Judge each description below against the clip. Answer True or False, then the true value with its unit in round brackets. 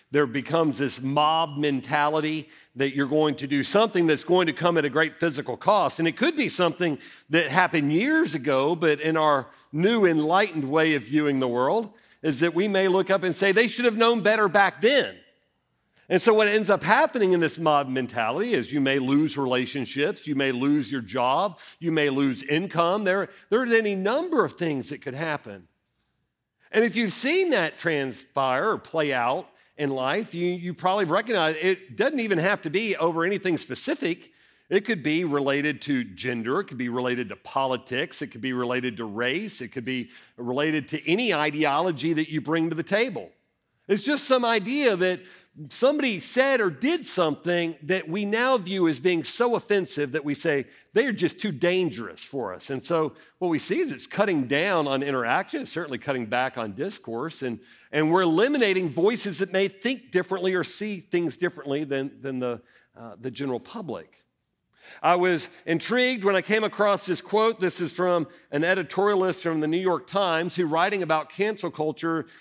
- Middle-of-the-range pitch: True (165 Hz)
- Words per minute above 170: True (190 wpm)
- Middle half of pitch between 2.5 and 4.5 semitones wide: False (5.3 semitones)